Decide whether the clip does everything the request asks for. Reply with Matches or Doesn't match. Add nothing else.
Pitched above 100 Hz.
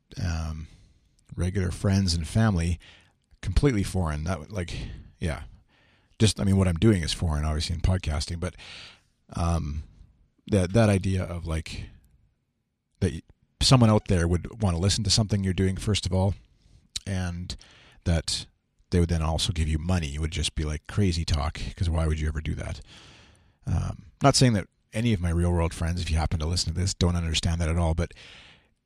Doesn't match